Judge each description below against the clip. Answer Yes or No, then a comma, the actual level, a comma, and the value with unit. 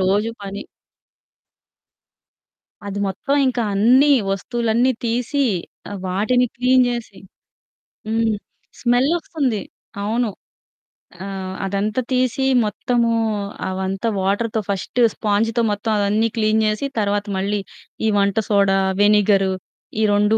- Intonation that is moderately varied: Yes, average, 3.2 semitones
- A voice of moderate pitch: No, high, 215 Hz